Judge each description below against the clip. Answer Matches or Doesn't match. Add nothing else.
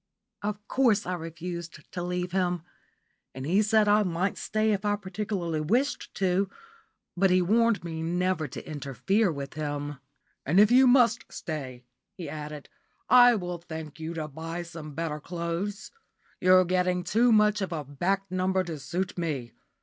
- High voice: Doesn't match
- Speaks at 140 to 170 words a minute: Matches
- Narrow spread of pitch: Doesn't match